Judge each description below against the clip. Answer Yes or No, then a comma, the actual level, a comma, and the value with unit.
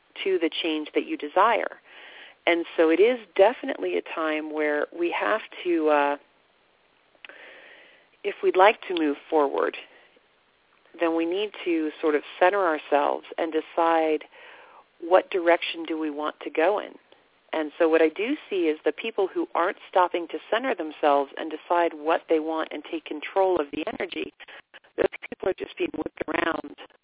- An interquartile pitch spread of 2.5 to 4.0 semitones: No, average, 4.5 semitones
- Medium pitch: Yes, medium, 165 Hz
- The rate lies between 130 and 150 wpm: No, average, 165 wpm